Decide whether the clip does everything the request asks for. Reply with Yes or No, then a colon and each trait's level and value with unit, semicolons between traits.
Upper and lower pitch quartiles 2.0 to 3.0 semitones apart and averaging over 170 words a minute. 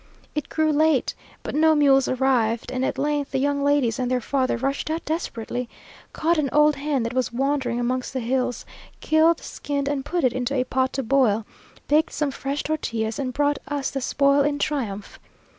Yes: narrow, 2.6 semitones; average, 190 wpm